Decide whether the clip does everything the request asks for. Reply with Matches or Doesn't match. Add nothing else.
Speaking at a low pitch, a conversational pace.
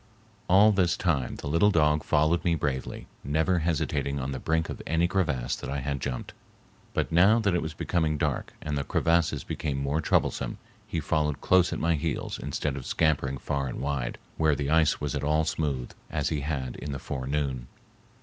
Matches